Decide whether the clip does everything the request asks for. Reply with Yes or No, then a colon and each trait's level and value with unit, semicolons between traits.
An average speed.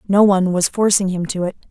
No: fast, 245 wpm